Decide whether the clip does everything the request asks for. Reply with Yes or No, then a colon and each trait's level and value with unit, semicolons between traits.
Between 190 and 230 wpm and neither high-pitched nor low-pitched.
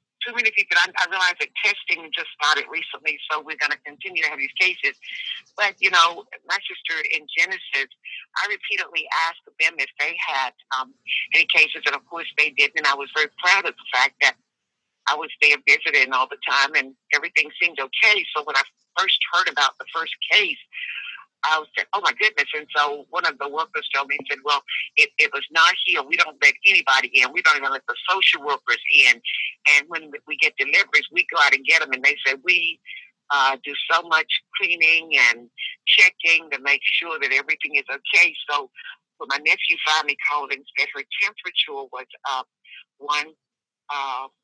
Yes: average, 200 wpm; medium, 155 Hz